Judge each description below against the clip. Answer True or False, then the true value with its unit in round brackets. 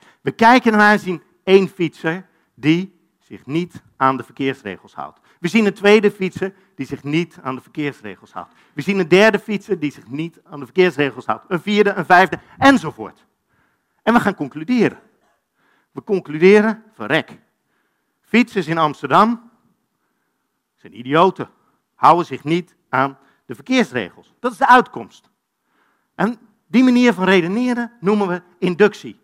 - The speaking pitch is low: False (185 Hz)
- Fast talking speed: False (150 wpm)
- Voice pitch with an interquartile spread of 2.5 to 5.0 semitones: False (5.5 semitones)